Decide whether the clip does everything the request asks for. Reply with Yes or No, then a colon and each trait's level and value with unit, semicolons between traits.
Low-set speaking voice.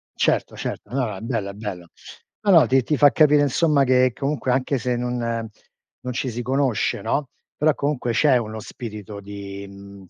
Yes: low, 125 Hz